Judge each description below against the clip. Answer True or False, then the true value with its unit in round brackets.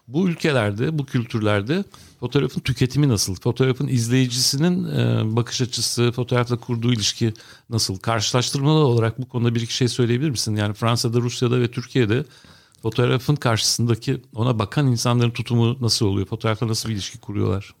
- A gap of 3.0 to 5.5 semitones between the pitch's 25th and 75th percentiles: False (2.4 semitones)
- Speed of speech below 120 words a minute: False (140 wpm)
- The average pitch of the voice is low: True (120 Hz)